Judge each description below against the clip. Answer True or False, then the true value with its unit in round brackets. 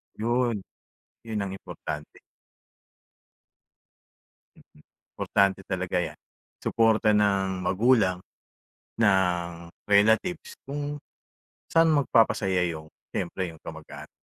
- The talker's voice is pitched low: True (100 Hz)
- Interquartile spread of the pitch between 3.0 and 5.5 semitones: True (3.7 semitones)